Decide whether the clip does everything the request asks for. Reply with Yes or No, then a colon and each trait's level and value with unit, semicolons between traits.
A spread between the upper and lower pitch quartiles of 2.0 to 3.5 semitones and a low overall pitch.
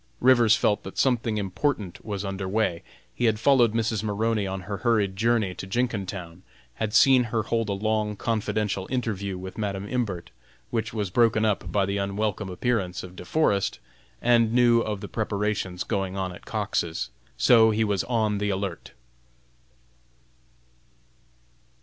Yes: average, 2.8 semitones; low, 105 Hz